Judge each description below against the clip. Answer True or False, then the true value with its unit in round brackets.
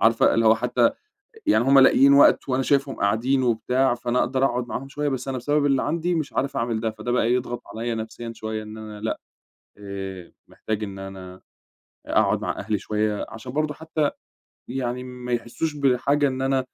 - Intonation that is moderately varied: True (3.7 semitones)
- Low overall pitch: True (125 Hz)